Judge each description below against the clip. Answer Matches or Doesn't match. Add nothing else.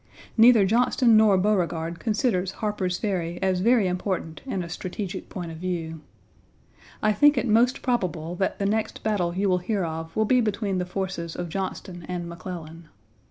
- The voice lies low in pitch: Doesn't match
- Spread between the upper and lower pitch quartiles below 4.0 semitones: Matches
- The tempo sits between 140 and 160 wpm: Doesn't match